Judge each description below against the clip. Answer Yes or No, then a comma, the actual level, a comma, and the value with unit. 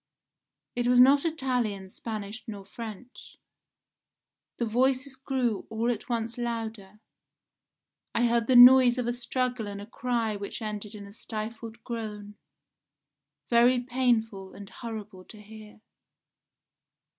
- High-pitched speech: Yes, high, 230 Hz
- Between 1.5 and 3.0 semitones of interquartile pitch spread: Yes, average, 2.7 semitones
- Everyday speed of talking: No, slow, 125 wpm